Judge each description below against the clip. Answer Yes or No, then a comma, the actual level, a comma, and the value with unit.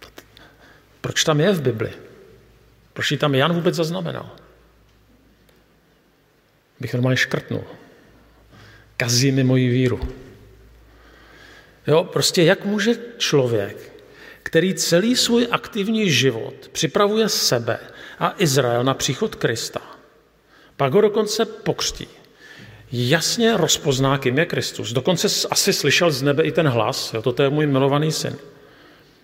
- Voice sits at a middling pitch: Yes, medium, 155 Hz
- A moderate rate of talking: Yes, average, 120 wpm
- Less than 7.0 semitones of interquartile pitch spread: No, wide, 7.5 semitones